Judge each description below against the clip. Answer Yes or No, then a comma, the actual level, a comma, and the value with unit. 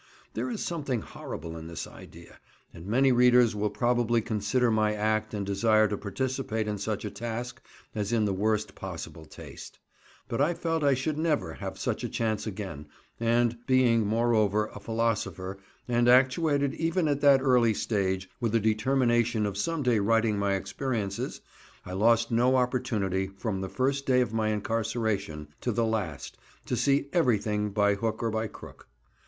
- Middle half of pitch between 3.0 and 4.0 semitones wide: Yes, average, 3.3 semitones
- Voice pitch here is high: No, low, 115 Hz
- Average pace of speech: Yes, average, 170 wpm